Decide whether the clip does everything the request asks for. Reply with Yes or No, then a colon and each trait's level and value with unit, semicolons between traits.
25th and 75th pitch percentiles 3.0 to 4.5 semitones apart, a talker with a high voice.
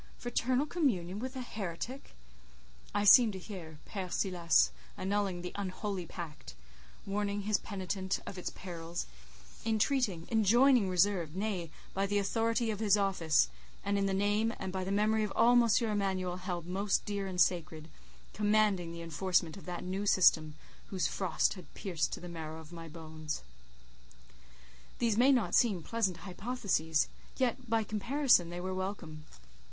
Yes: average, 3.6 semitones; high, 195 Hz